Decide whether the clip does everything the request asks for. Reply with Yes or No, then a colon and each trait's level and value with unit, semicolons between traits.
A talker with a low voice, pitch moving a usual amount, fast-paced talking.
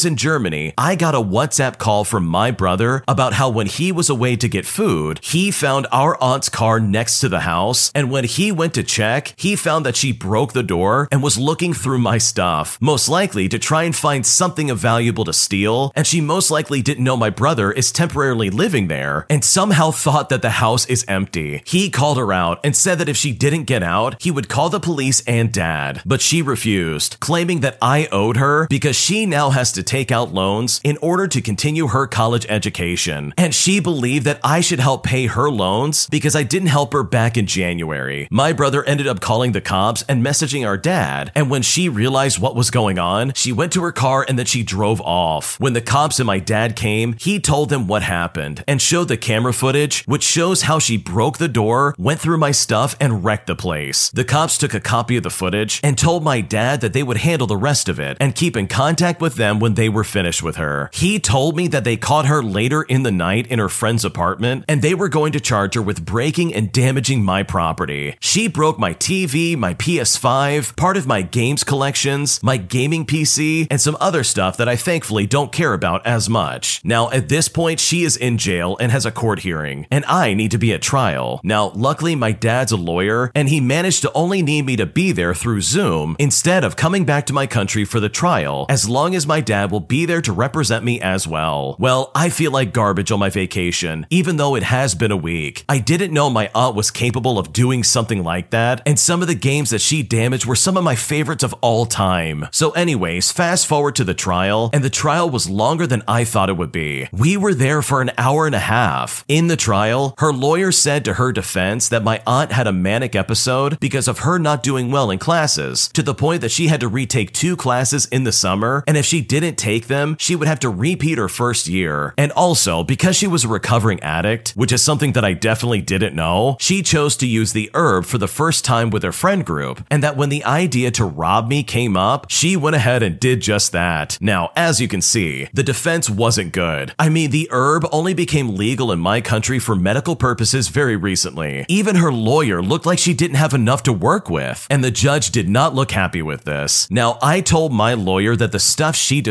No: low, 125 Hz; wide, 5.8 semitones; fast, 230 wpm